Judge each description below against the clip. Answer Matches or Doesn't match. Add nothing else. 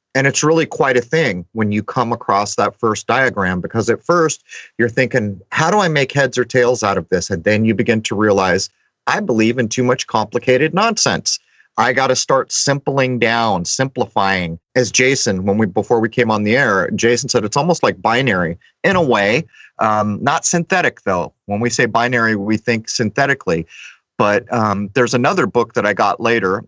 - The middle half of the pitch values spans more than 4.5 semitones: Doesn't match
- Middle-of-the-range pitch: Doesn't match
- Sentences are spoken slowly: Doesn't match